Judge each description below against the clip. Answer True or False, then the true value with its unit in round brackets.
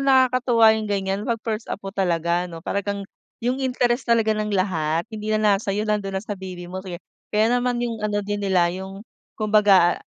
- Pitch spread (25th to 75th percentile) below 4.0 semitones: True (2.8 semitones)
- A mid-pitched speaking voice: False (205 Hz)